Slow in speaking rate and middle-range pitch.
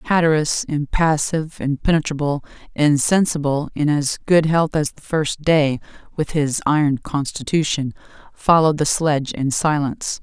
Yes: slow, 125 wpm; medium, 150 Hz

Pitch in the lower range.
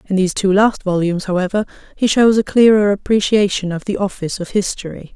No: high, 200 Hz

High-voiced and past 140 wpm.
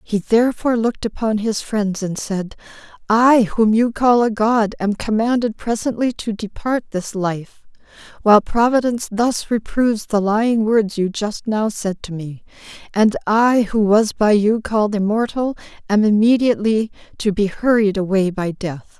Yes: high, 215 Hz; average, 160 wpm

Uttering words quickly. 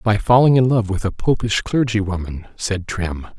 No: average, 195 wpm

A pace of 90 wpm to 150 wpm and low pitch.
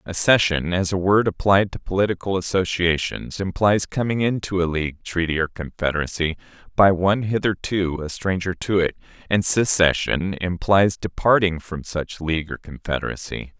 Yes: average, 140 wpm; very low, 90 Hz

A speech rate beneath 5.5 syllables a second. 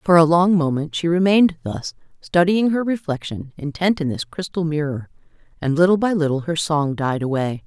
Yes: 5.3 syllables/s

